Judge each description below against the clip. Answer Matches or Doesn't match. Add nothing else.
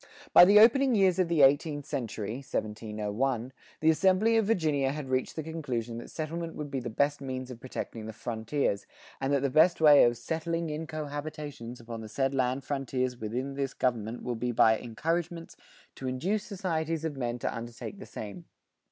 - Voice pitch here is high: Doesn't match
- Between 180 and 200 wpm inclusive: Matches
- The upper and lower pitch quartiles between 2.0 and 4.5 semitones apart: Doesn't match